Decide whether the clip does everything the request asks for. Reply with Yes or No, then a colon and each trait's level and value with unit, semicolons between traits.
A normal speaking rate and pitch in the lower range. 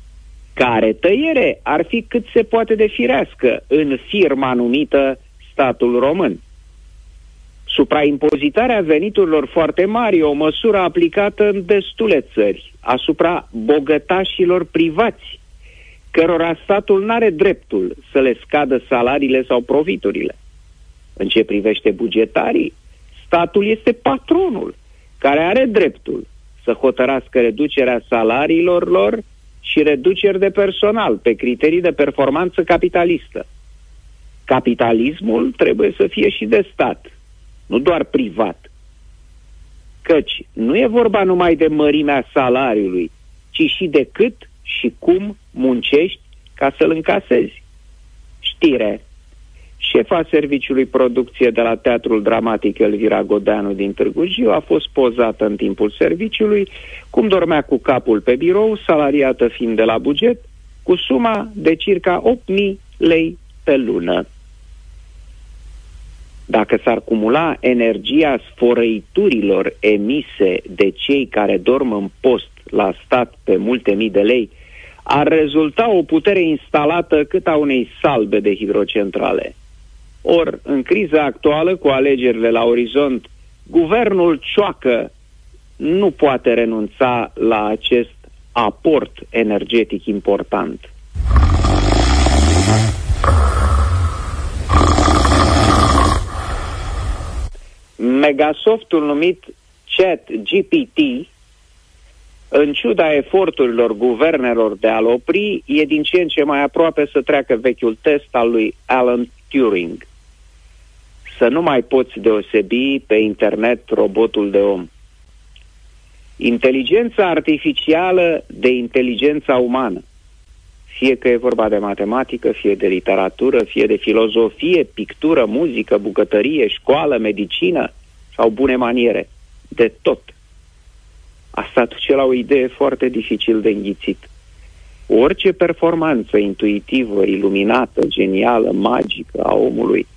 No: slow, 110 wpm; low, 125 Hz